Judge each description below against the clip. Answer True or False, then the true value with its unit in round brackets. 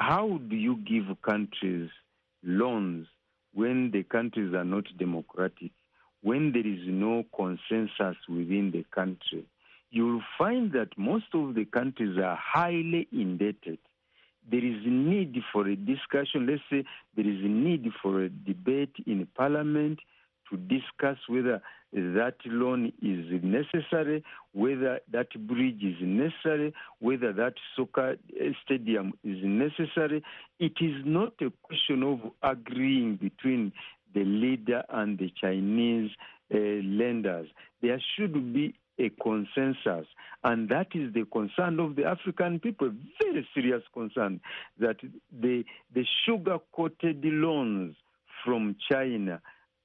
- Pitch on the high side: False (125 Hz)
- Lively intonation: True (7.4 semitones)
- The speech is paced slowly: True (130 wpm)